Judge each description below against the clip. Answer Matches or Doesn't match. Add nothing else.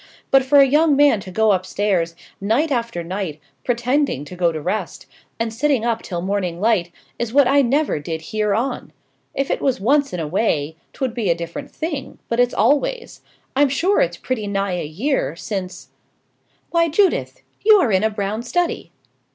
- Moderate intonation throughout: Doesn't match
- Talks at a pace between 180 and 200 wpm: Matches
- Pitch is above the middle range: Matches